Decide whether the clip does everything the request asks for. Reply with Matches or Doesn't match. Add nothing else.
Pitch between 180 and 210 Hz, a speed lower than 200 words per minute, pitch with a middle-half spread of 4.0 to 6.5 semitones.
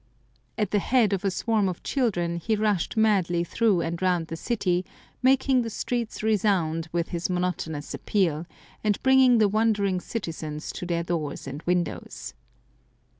Matches